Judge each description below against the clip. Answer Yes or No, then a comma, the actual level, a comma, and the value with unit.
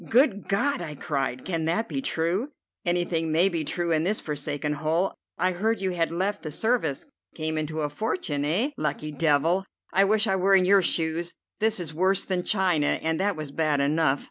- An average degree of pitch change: Yes, average, 4.0 semitones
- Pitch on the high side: No, medium, 170 Hz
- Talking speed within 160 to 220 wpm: Yes, average, 195 wpm